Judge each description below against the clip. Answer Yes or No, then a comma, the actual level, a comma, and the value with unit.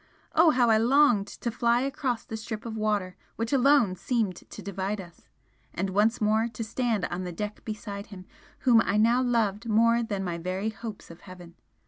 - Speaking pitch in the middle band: No, high, 220 Hz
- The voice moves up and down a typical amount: Yes, average, 3.2 semitones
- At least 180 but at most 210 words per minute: Yes, average, 190 wpm